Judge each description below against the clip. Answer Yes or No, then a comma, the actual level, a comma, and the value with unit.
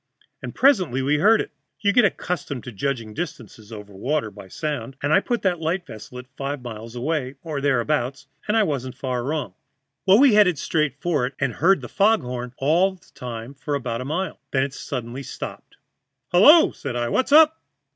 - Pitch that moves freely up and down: Yes, wide, 6.3 semitones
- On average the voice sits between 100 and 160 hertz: Yes, medium, 140 Hz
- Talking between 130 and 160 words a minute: No, average, 200 wpm